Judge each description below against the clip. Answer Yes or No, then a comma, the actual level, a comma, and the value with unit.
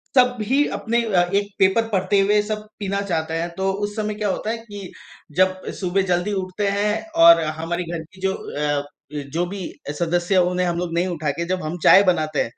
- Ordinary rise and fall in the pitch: Yes, average, 3.1 semitones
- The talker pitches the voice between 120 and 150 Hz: No, medium, 185 Hz